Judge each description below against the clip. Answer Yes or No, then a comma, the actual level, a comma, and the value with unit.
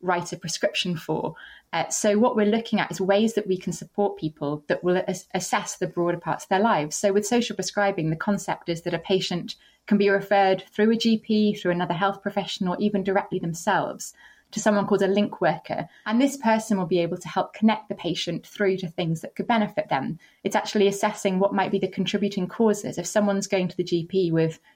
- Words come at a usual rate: No, fast, 220 wpm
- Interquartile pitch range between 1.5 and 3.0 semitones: Yes, average, 2.7 semitones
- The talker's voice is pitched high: Yes, high, 195 Hz